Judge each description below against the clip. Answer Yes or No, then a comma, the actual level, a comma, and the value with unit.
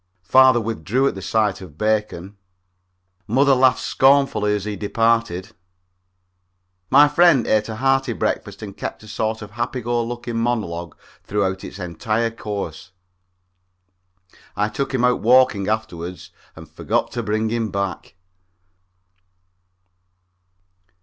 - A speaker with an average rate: No, slow, 130 wpm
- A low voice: Yes, low, 110 Hz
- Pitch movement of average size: Yes, average, 3.5 semitones